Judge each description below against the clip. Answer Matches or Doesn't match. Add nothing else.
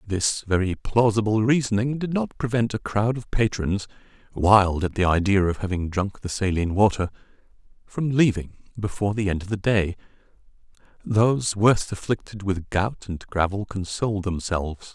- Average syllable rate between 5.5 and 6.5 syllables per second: Doesn't match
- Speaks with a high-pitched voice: Doesn't match